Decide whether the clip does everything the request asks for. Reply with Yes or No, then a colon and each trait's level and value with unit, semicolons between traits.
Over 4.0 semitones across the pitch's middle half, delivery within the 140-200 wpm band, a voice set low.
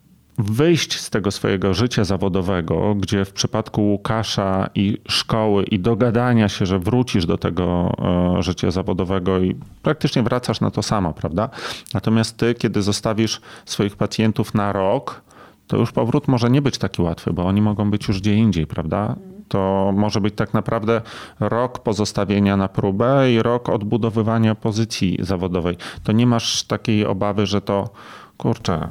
No: average, 2.8 semitones; average, 155 wpm; low, 105 Hz